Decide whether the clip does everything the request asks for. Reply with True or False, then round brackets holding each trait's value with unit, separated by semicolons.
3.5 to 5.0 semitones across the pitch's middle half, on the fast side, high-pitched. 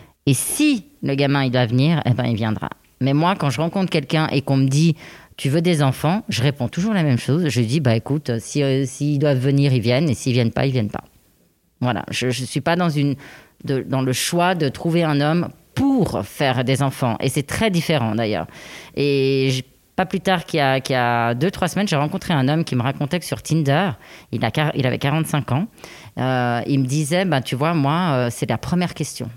False (4.3 semitones; 240 wpm; 140 Hz)